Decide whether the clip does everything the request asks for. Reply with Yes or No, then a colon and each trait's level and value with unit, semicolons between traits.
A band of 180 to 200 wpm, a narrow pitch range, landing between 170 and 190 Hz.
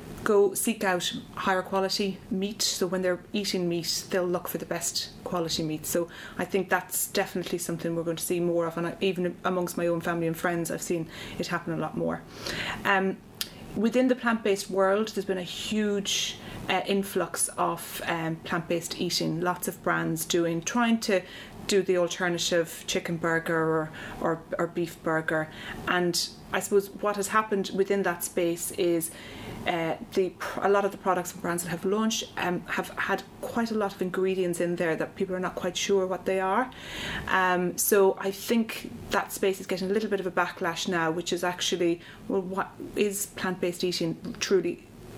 Yes: average, 190 wpm; narrow, 2.3 semitones; medium, 185 Hz